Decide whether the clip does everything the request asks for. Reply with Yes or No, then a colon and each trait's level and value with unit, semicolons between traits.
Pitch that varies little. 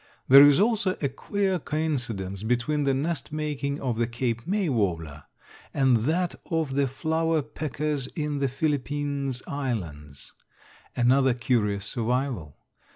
No: average, 4.3 semitones